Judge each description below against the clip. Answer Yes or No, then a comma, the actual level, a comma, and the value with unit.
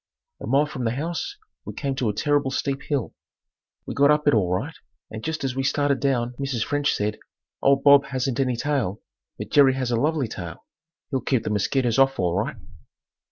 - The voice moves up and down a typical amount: Yes, average, 3.3 semitones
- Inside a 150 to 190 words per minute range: No, fast, 205 wpm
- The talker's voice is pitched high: No, low, 135 Hz